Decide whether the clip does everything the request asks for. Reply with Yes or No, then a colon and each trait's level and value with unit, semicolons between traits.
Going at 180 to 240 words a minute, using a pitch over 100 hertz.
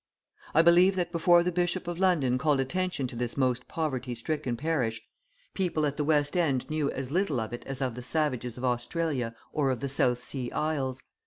Yes: average, 195 wpm; medium, 140 Hz